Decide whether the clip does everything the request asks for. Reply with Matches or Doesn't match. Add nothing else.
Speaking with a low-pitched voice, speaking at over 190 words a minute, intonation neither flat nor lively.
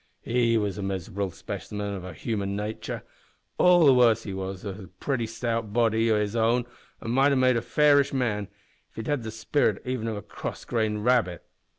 Matches